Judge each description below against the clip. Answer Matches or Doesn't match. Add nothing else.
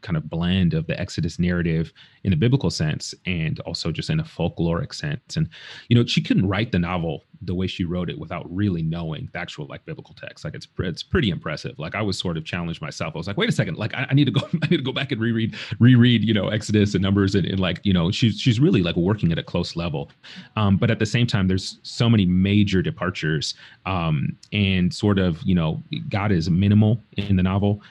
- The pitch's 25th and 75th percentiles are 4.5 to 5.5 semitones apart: Matches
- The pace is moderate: Doesn't match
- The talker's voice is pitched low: Matches